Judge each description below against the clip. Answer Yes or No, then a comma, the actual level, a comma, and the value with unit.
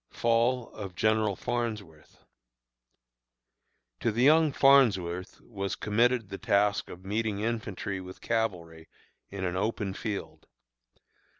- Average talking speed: No, slow, 110 wpm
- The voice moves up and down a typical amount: Yes, average, 3.4 semitones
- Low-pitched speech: Yes, low, 105 Hz